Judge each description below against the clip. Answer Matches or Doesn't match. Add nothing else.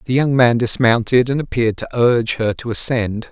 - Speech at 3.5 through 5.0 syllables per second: Doesn't match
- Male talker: Matches